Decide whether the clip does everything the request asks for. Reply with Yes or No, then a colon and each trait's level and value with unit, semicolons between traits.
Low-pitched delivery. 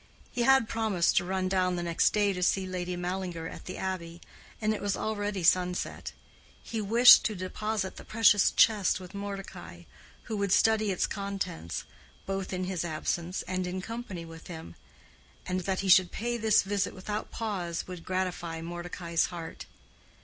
No: medium, 185 Hz